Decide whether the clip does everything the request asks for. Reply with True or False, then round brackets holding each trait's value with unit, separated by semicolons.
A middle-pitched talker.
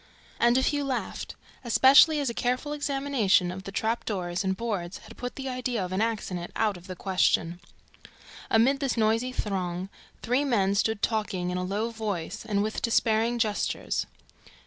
False (220 Hz)